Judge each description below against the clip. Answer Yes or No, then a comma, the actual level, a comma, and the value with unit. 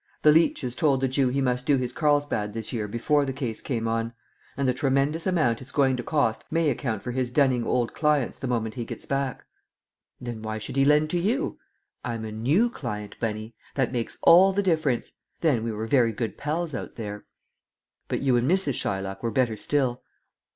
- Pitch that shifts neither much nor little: Yes, average, 4.2 semitones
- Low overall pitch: Yes, low, 130 Hz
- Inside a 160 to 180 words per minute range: No, fast, 205 wpm